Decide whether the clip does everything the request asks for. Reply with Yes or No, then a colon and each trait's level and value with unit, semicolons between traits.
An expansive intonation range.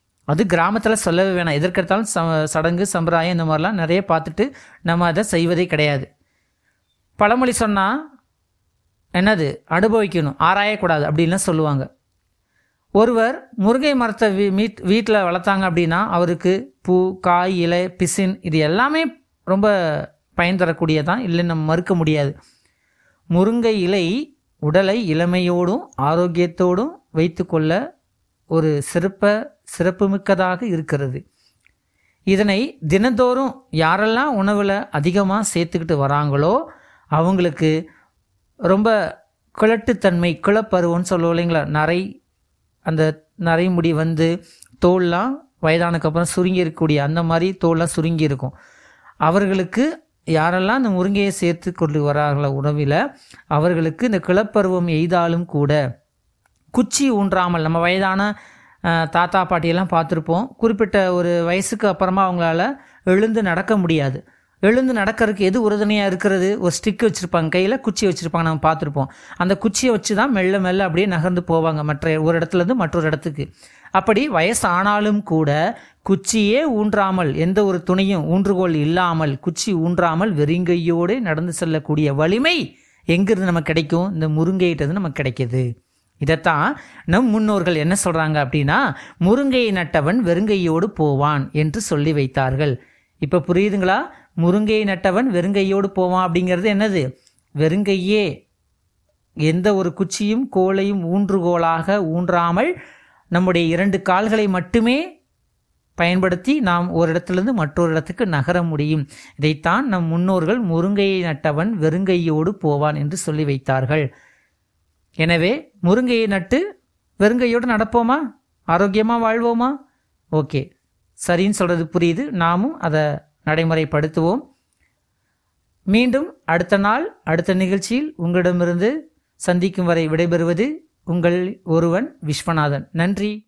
No: average, 4.0 semitones